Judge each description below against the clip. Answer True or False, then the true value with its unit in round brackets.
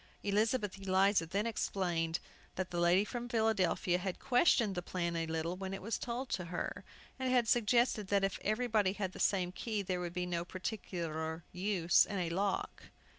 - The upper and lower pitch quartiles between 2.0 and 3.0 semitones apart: False (3.5 semitones)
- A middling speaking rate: True (175 wpm)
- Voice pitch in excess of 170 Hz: True (190 Hz)